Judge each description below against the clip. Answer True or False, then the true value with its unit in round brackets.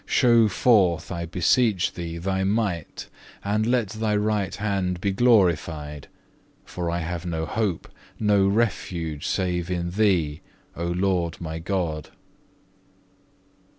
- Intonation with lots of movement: False (3.7 semitones)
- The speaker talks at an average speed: False (120 wpm)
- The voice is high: False (90 Hz)